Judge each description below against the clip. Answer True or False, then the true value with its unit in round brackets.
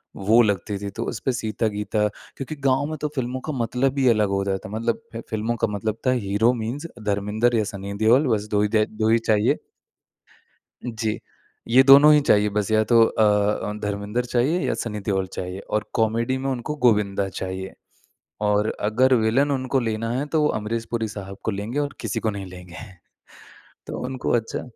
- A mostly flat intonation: False (3.4 semitones)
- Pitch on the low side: True (110 Hz)